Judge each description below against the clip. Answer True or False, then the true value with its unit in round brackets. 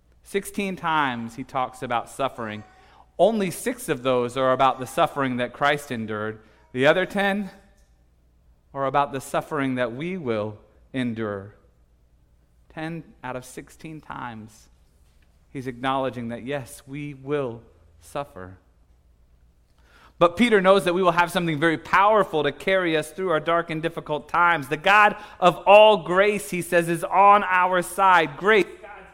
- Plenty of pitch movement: True (8.2 semitones)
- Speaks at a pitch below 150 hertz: True (140 Hz)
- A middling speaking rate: True (145 wpm)